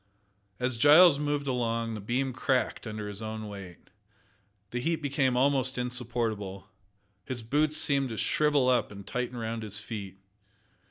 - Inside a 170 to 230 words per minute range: No, average, 150 wpm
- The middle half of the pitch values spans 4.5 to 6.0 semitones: No, average, 3.9 semitones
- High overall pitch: No, low, 125 Hz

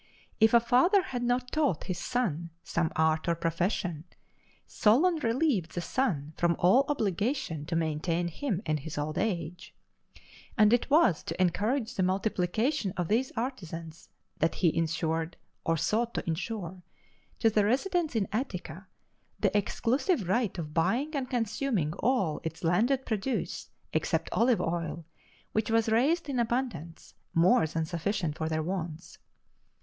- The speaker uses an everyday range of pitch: No, wide, 6.8 semitones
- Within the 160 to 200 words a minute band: No, average, 145 wpm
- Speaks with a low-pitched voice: No, high, 195 Hz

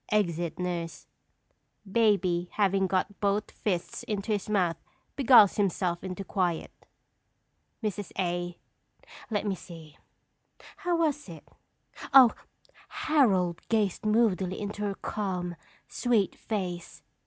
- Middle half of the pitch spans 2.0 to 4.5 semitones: Yes, average, 3.2 semitones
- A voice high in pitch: Yes, high, 195 Hz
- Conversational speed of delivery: No, slow, 110 wpm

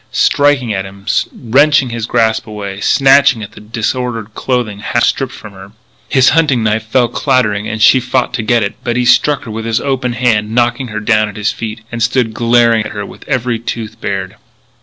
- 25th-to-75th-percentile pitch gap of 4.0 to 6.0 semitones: No, average, 2.8 semitones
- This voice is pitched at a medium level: No, low, 115 Hz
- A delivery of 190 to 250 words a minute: Yes, average, 200 wpm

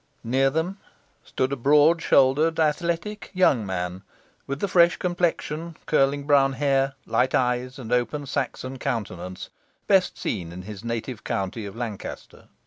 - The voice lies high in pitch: No, low, 135 Hz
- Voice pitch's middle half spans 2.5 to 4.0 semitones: No, average, 5.0 semitones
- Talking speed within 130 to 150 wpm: Yes, average, 140 wpm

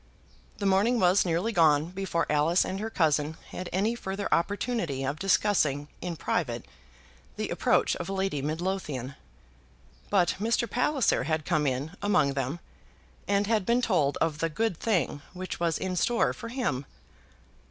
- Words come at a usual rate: Yes, average, 150 wpm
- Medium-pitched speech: Yes, medium, 180 Hz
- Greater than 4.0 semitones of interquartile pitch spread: Yes, average, 5.2 semitones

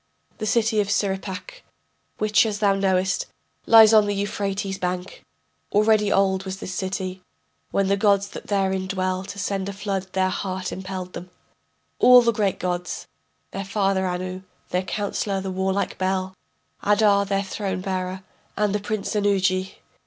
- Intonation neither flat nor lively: No, narrow, 1.5 semitones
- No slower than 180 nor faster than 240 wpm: No, average, 150 wpm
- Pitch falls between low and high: No, high, 195 Hz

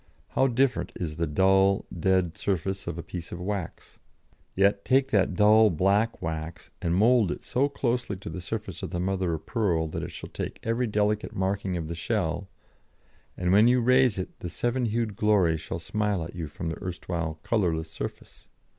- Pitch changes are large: No, average, 4.1 semitones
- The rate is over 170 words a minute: Yes, average, 190 wpm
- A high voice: No, very low, 95 Hz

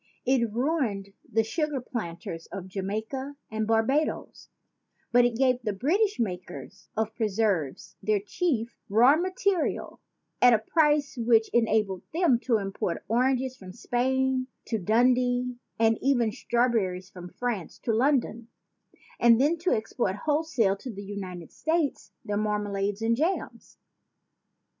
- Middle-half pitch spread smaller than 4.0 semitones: No, average, 4.3 semitones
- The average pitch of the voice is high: Yes, high, 230 Hz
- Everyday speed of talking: No, slow, 130 wpm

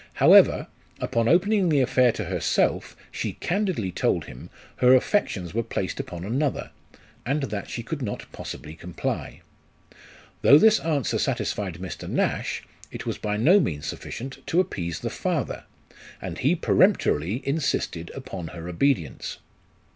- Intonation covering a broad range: Yes, wide, 8.3 semitones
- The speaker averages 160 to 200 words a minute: No, average, 140 wpm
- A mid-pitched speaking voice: No, low, 115 Hz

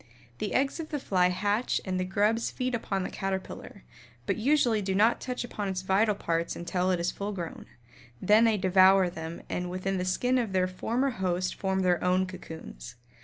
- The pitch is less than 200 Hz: Yes, high, 190 Hz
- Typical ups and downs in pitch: Yes, average, 3.0 semitones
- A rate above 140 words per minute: Yes, average, 195 wpm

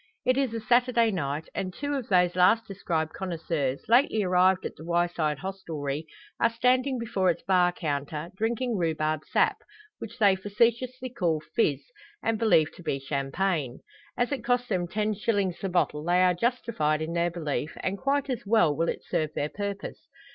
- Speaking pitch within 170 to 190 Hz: Yes, medium, 185 Hz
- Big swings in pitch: Yes, wide, 6.2 semitones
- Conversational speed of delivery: Yes, average, 175 wpm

